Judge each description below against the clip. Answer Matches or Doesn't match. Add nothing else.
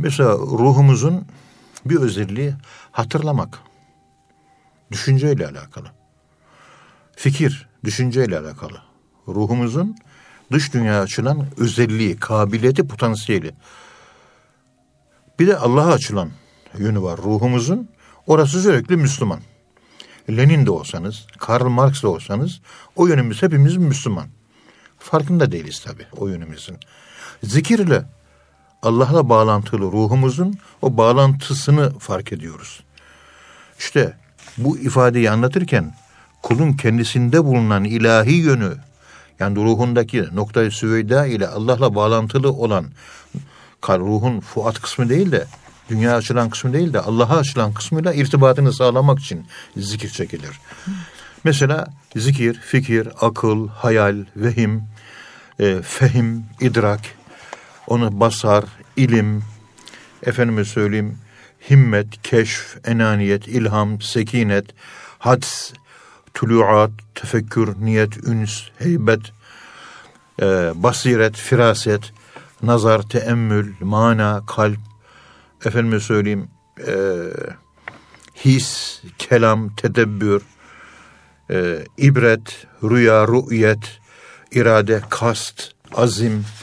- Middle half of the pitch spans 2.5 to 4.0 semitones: Matches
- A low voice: Matches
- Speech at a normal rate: Doesn't match